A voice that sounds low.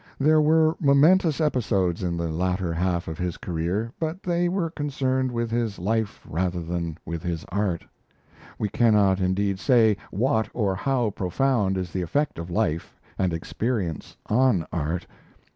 Yes: low, 100 Hz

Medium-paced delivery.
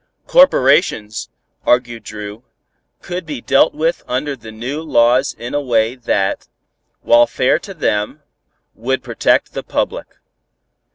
No: slow, 125 wpm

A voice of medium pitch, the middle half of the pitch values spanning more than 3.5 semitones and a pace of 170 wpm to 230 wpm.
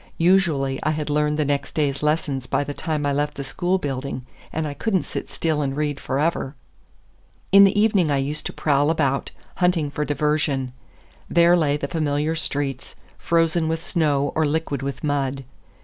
No: medium, 150 Hz; narrow, 2.5 semitones; average, 180 wpm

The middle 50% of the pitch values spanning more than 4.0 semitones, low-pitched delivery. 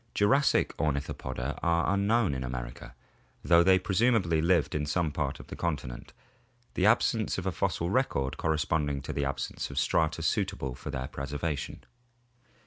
Yes: wide, 5.4 semitones; very low, 80 Hz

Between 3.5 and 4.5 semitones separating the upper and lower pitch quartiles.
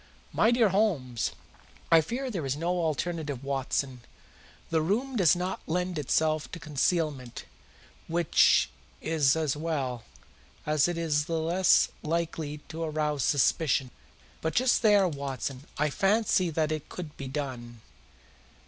Yes: average, 3.8 semitones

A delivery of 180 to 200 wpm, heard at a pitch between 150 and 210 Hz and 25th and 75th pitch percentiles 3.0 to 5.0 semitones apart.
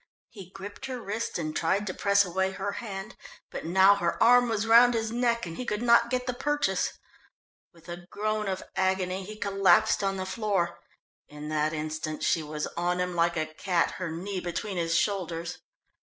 Yes: average, 190 wpm; high, 190 Hz; average, 3.8 semitones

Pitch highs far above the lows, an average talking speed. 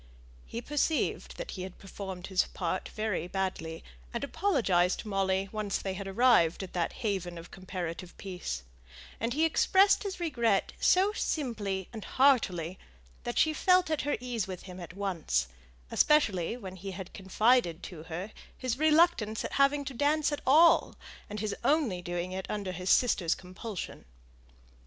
Yes: wide, 6.8 semitones; average, 160 wpm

